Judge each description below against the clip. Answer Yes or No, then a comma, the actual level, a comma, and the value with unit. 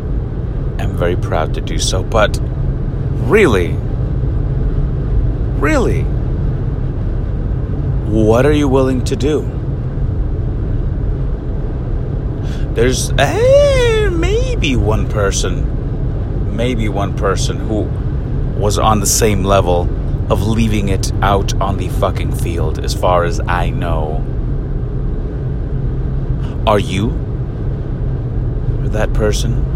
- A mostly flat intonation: No, average, 3.5 semitones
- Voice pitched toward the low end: Yes, low, 120 Hz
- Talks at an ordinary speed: No, slow, 95 wpm